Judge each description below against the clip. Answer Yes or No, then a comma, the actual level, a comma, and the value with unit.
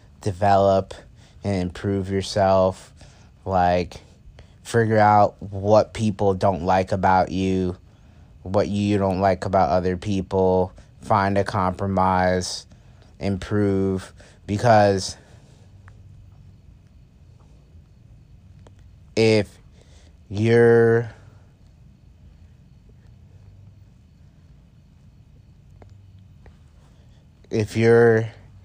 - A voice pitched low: Yes, low, 100 Hz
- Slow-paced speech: Yes, slow, 60 wpm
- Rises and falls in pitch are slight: Yes, narrow, 2.1 semitones